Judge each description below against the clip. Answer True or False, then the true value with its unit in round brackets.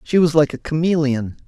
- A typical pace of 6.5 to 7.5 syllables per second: False (5.4 syllables/s)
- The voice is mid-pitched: True (150 Hz)